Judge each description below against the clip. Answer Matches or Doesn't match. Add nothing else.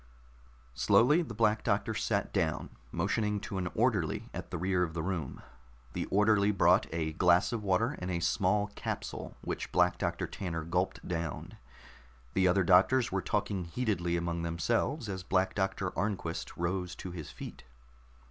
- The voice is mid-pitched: Doesn't match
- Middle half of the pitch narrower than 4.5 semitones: Matches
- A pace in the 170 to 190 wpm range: Doesn't match